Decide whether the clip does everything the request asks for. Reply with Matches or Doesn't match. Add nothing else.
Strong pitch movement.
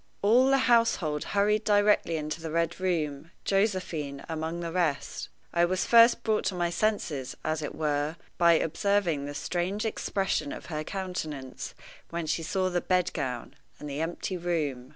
Doesn't match